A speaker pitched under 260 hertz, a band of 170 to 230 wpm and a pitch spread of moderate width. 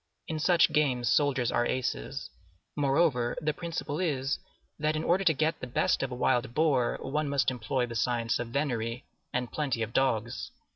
Yes: low, 135 Hz; average, 180 wpm; average, 3.9 semitones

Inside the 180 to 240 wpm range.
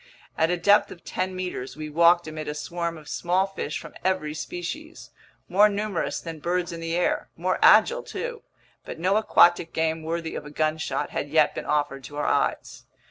Yes: average, 190 wpm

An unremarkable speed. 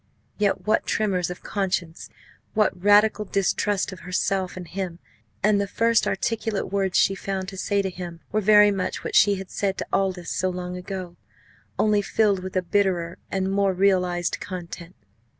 Yes: average, 170 wpm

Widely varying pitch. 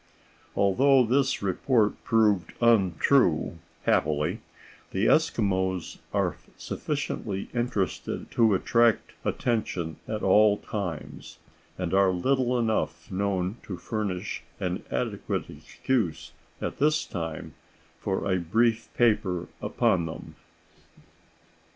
No: average, 4.4 semitones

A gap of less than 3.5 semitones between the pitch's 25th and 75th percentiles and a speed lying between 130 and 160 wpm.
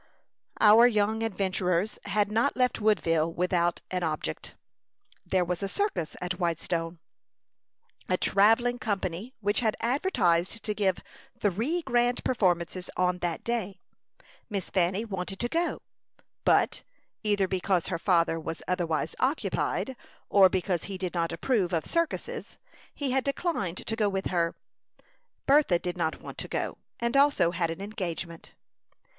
No: average, 4.5 semitones; average, 140 wpm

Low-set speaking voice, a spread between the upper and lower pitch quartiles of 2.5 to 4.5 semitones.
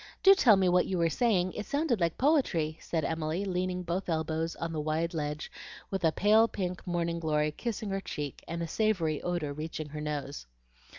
No: medium, 170 Hz; average, 3.7 semitones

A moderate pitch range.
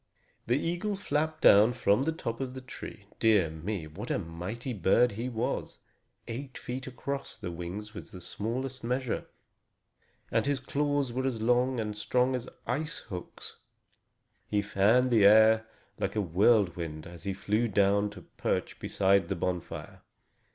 Yes: average, 4.6 semitones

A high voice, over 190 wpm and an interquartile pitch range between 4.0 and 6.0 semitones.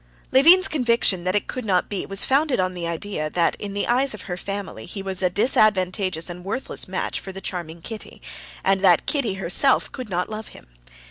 Yes: high, 195 Hz; fast, 205 wpm; average, 4.4 semitones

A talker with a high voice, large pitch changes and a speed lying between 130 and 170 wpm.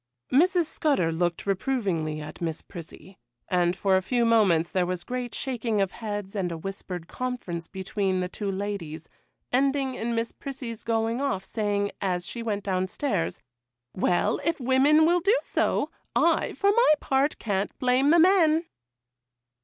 Yes: high, 210 Hz; wide, 6.2 semitones; average, 160 wpm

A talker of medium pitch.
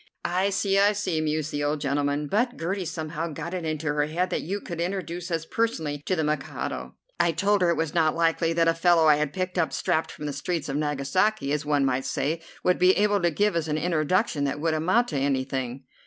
Yes: medium, 160 Hz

